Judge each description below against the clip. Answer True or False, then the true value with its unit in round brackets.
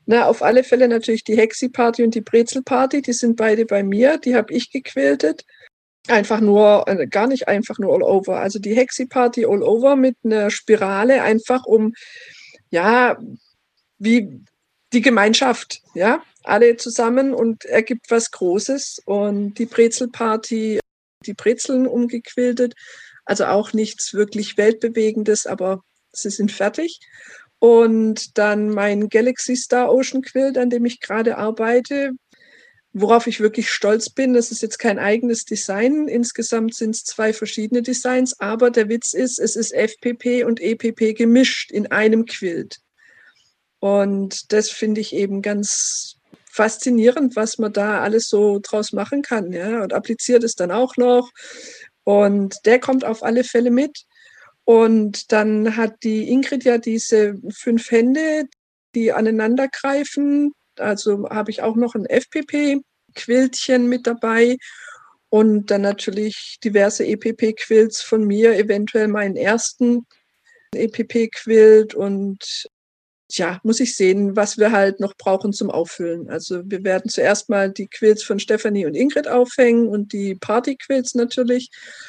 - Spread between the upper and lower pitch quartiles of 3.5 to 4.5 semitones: False (2.8 semitones)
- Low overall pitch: False (225 Hz)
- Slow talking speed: False (145 wpm)